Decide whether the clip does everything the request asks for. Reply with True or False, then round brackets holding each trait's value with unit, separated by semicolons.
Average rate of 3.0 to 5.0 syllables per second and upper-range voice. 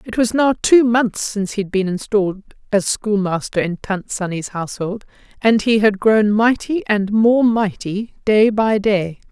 True (4.4 syllables/s; 210 Hz)